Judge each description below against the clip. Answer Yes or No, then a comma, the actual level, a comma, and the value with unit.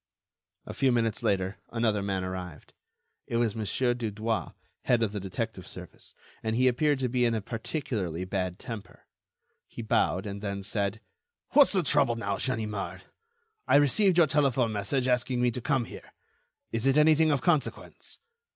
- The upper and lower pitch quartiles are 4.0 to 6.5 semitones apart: Yes, average, 4.6 semitones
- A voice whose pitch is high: No, low, 115 Hz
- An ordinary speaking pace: Yes, average, 165 wpm